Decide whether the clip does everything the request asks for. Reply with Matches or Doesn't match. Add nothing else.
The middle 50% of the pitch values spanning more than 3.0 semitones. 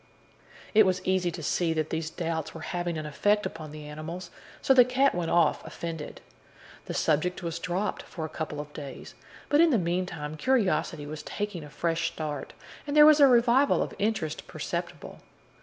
Matches